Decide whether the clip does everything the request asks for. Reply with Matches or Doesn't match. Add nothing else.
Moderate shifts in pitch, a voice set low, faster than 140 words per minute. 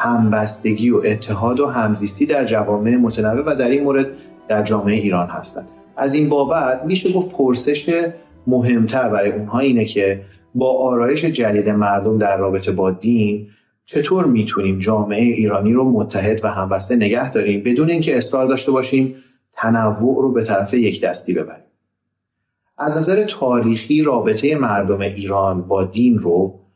Matches